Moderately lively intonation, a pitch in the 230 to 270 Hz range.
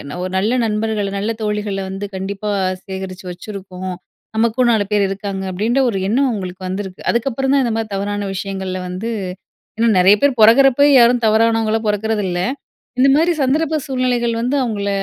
No: average, 3.4 semitones; high, 215 Hz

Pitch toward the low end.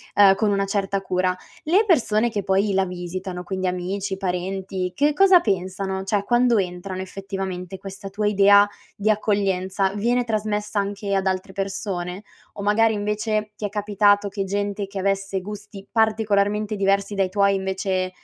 No: high, 200 Hz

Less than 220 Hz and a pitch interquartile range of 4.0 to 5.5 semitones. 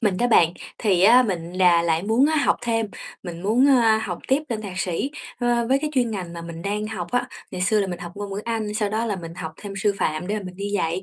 Yes: high, 205 Hz; average, 4.4 semitones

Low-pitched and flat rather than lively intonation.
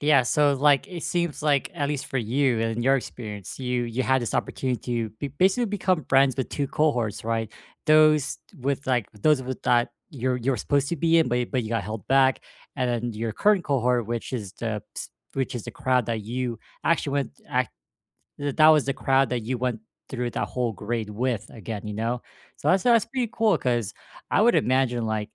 No: low, 130 Hz; average, 3.6 semitones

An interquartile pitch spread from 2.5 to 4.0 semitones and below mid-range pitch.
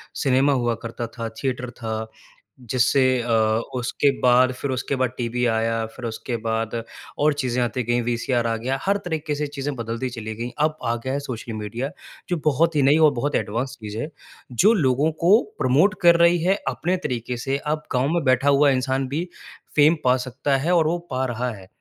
Yes: average, 3.6 semitones; low, 130 Hz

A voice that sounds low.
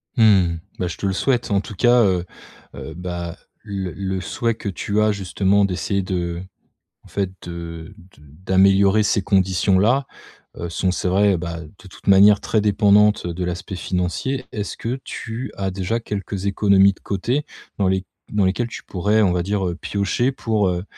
Yes: very low, 95 Hz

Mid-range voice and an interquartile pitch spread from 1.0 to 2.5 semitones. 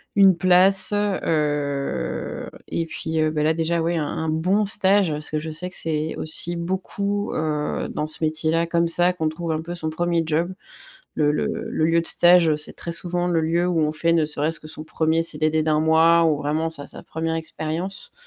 Yes: medium, 160 Hz; narrow, 1.9 semitones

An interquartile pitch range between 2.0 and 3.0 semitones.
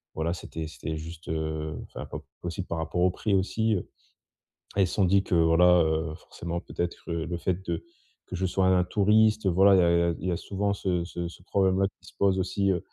Yes: narrow, 2.4 semitones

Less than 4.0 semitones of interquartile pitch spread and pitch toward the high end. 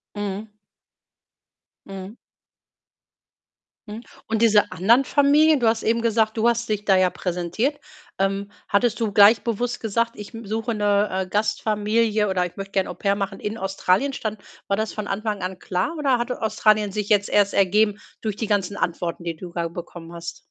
Yes: narrow, 2.6 semitones; high, 210 Hz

